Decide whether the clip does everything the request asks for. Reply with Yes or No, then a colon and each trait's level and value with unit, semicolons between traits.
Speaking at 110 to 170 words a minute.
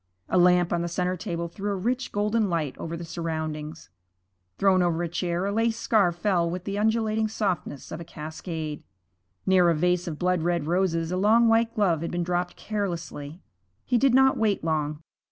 No: average, 190 wpm